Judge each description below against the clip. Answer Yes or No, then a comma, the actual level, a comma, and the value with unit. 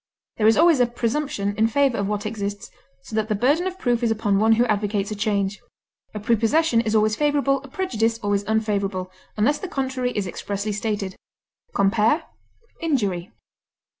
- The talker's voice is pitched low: No, high, 220 Hz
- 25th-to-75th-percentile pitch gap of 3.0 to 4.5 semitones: Yes, average, 3.9 semitones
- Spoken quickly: No, average, 170 wpm